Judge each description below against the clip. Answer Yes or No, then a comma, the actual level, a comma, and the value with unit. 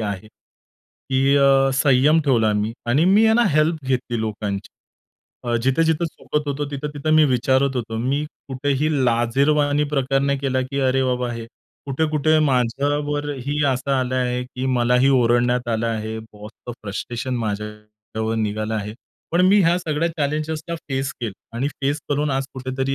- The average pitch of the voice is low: Yes, low, 130 Hz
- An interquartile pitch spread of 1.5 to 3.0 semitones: No, average, 3.8 semitones